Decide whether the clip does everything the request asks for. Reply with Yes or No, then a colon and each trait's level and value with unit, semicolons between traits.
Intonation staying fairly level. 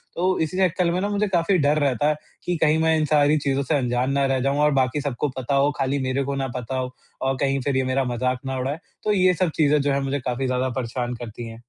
No: average, 3.1 semitones